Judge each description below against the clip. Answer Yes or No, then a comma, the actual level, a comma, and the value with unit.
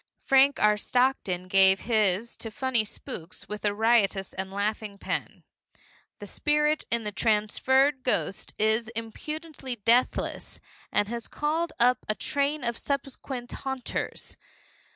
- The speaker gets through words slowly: Yes, slow, 130 wpm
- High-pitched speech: Yes, high, 235 Hz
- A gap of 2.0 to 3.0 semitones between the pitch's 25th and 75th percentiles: No, average, 4.2 semitones